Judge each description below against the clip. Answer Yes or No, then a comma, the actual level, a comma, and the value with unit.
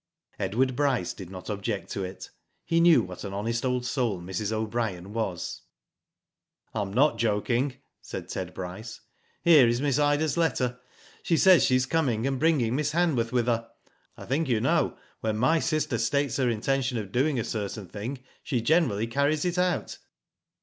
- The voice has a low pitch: Yes, low, 120 Hz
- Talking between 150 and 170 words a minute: No, average, 180 wpm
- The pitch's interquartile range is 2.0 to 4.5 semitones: No, average, 5.2 semitones